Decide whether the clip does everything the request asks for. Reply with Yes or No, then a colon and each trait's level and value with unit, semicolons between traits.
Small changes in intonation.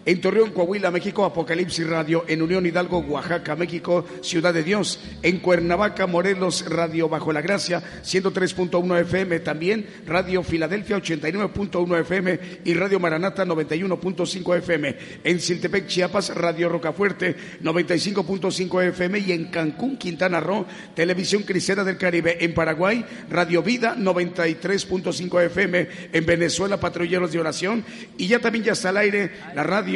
Yes: narrow, 2.3 semitones